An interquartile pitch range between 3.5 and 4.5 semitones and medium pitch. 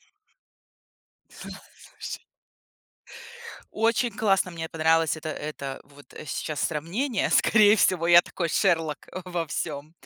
Yes: average, 3.9 semitones; medium, 165 Hz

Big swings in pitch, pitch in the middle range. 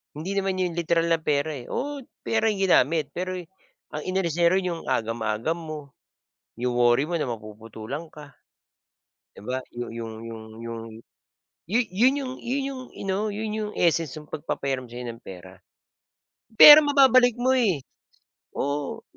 Yes: wide, 9.0 semitones; medium, 165 Hz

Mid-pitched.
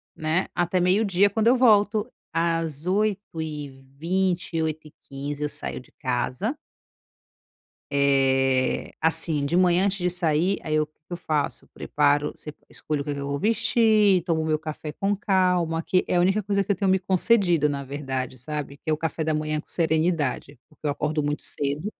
Yes: medium, 160 Hz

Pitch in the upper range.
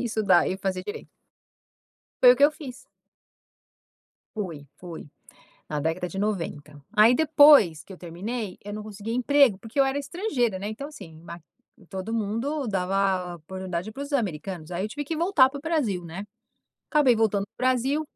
Yes: high, 210 Hz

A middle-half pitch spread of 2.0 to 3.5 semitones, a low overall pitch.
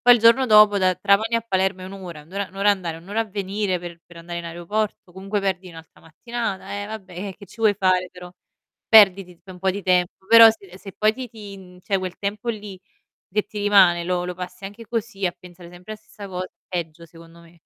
No: narrow, 2.6 semitones; high, 190 Hz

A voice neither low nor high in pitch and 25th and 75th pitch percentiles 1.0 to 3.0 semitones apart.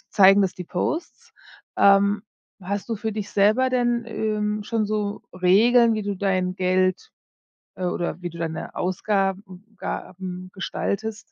No: high, 200 Hz; average, 2.7 semitones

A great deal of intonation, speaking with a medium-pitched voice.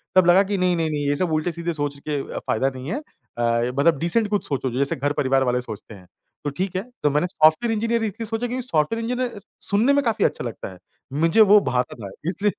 Yes: wide, 7.0 semitones; medium, 170 Hz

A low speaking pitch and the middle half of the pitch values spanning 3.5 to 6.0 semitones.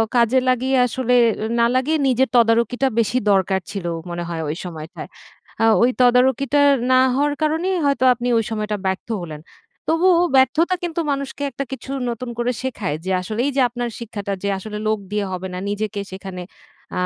No: high, 235 Hz; average, 4.7 semitones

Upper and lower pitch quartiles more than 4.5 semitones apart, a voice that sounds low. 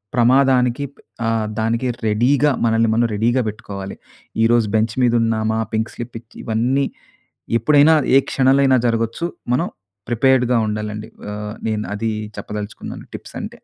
No: average, 2.8 semitones; low, 115 Hz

